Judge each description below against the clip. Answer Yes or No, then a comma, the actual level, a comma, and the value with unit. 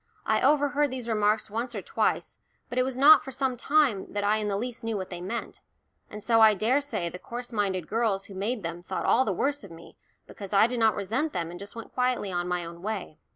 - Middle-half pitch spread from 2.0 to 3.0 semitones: No, average, 4.5 semitones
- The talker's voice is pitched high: Yes, high, 220 Hz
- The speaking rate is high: Yes, fast, 245 wpm